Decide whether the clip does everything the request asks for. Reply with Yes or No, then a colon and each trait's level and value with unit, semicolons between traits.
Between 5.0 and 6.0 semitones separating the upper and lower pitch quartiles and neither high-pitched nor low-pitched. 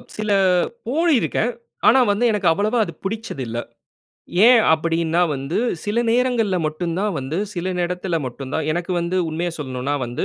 Yes: wide, 5.6 semitones; medium, 175 Hz